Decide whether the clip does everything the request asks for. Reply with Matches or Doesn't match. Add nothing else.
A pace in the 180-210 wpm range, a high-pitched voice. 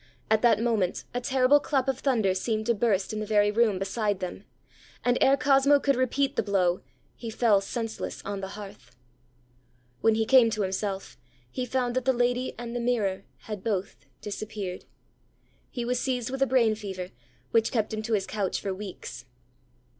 Matches